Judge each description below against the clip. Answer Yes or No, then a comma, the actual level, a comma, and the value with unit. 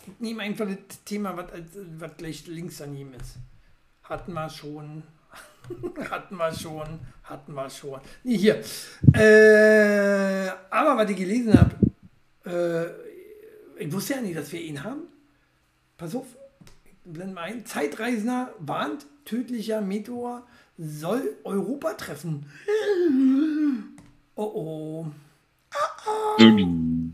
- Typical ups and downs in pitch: No, wide, 7.7 semitones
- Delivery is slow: Yes, slow, 120 wpm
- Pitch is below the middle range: No, high, 195 Hz